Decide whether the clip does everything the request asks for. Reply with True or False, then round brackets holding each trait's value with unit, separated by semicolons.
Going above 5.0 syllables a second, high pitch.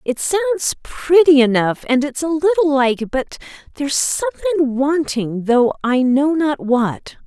False (4.5 syllables/s; 285 Hz)